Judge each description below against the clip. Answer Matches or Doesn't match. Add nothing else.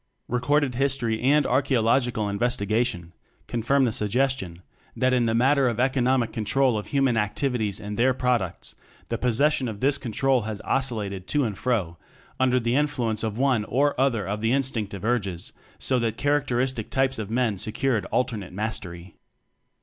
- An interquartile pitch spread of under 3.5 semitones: Doesn't match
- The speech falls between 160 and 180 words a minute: Matches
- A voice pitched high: Doesn't match